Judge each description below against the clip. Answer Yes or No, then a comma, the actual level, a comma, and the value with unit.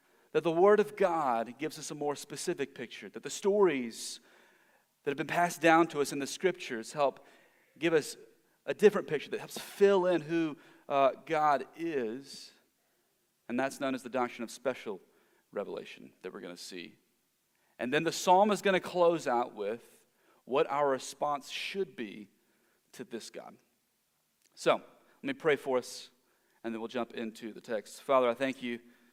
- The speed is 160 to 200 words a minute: Yes, average, 180 wpm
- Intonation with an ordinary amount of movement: No, wide, 6.4 semitones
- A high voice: No, medium, 145 Hz